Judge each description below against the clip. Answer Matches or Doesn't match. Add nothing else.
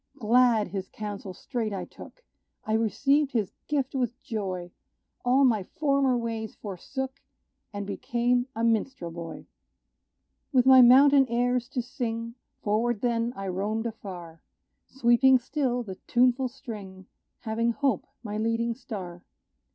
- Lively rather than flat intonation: Doesn't match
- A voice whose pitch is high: Matches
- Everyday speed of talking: Doesn't match